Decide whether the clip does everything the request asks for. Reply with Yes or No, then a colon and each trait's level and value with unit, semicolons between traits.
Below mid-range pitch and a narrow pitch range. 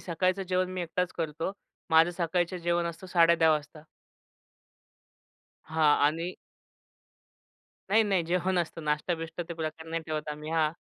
No: medium, 170 Hz; narrow, 2.1 semitones